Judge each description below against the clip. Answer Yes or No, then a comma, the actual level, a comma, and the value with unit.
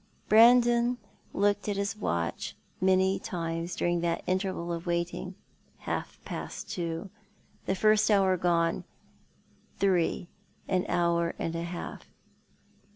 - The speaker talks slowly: Yes, slow, 125 wpm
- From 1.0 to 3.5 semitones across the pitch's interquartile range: Yes, average, 2.9 semitones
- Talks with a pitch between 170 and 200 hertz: Yes, medium, 185 Hz